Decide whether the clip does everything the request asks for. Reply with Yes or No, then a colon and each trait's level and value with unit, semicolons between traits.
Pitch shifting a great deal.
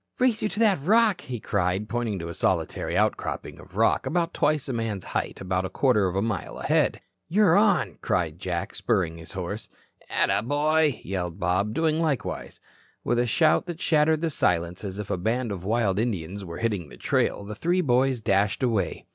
Yes: wide, 8.5 semitones